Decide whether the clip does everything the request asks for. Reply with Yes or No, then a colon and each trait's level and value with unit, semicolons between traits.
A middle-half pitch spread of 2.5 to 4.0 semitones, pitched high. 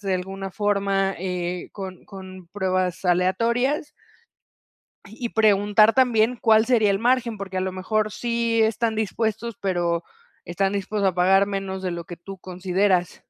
Yes: average, 2.9 semitones; high, 195 Hz